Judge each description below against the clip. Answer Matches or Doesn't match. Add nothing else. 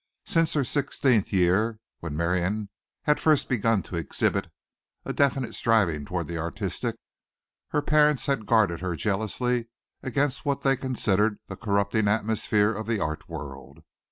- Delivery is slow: Doesn't match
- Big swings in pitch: Matches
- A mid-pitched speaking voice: Doesn't match